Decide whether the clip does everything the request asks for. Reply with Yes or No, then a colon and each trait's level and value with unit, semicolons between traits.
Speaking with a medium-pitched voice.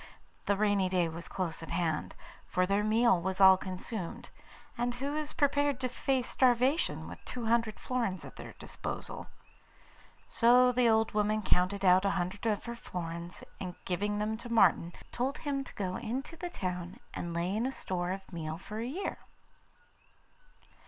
No: high, 210 Hz